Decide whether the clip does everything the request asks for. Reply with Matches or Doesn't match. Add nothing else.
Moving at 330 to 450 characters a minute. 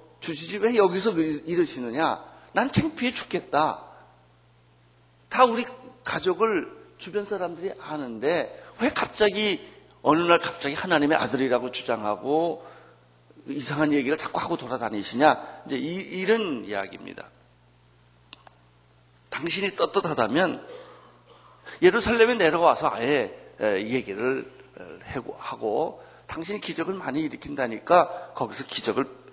Doesn't match